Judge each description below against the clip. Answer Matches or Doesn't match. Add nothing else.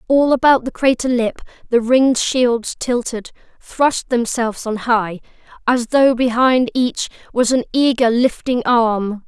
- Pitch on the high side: Matches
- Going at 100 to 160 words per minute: Matches